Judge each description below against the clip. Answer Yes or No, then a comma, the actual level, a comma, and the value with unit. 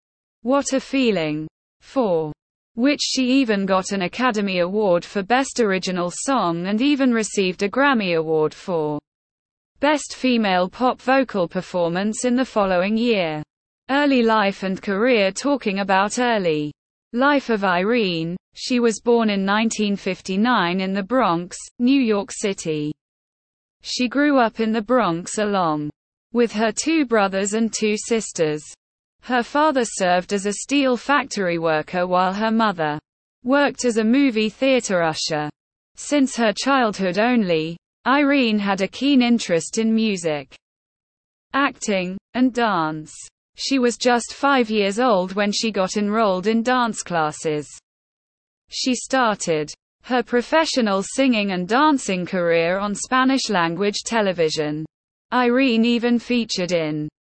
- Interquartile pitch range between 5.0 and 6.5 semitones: Yes, wide, 5.6 semitones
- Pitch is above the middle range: Yes, high, 210 Hz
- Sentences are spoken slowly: Yes, slow, 130 wpm